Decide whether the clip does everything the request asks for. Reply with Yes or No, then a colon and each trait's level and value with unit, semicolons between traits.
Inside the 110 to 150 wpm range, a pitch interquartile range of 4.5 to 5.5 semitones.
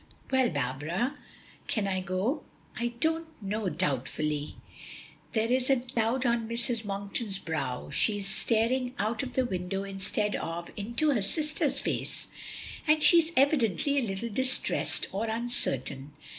Yes: average, 145 wpm; average, 5.2 semitones